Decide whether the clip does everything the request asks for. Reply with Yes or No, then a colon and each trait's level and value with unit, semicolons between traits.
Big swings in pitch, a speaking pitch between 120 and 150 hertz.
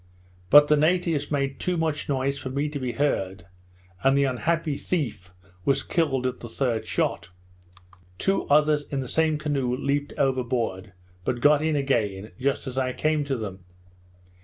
No: average, 3.1 semitones; medium, 140 Hz